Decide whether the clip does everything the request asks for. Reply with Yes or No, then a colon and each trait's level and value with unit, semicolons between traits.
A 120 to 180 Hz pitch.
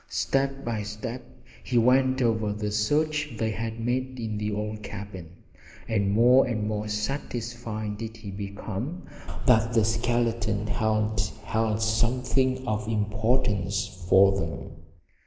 No: low, 110 Hz